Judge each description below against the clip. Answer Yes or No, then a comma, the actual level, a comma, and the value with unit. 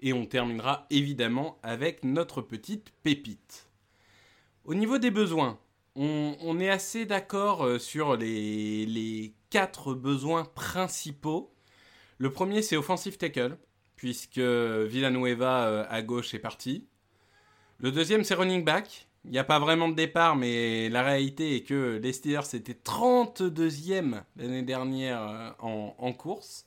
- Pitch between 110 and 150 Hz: Yes, low, 135 Hz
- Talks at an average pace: No, slow, 135 wpm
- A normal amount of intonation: No, wide, 6.0 semitones